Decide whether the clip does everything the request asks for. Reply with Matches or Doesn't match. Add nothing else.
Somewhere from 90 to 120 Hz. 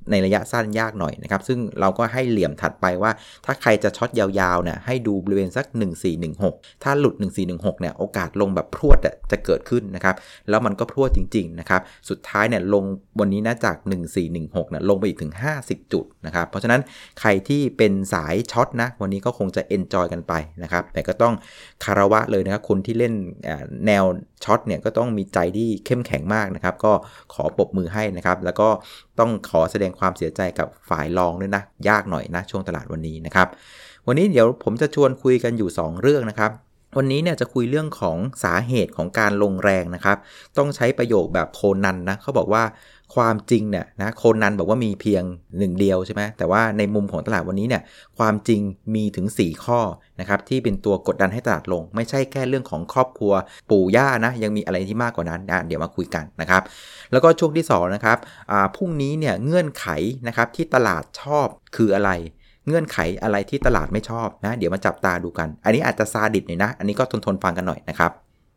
Matches